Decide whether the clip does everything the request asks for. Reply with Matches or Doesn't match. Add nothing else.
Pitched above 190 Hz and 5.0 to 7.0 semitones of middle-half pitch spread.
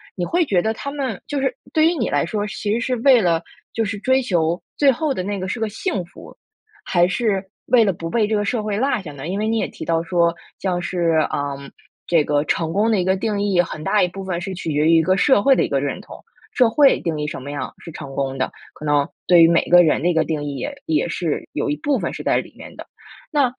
Doesn't match